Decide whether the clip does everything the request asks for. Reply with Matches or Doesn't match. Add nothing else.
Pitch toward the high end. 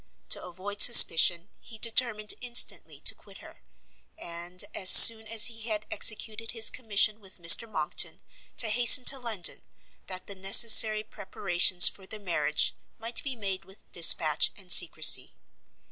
Matches